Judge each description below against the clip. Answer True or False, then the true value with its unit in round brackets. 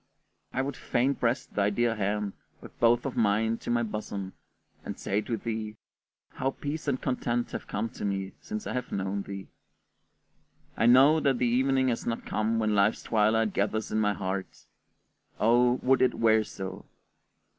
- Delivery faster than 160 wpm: True (175 wpm)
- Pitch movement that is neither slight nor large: True (3.2 semitones)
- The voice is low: True (115 Hz)